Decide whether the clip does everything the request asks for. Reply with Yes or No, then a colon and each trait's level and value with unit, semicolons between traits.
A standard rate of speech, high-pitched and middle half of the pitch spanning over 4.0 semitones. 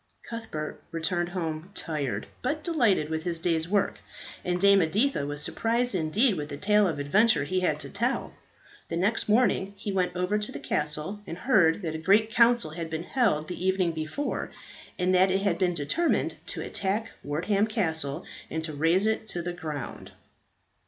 No: average, 180 wpm; medium, 180 Hz; average, 4.8 semitones